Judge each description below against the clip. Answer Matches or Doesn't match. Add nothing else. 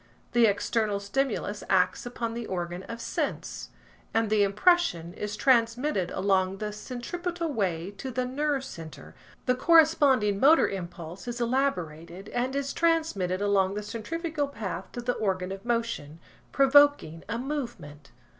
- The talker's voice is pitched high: Matches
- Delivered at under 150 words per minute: Matches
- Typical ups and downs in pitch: Doesn't match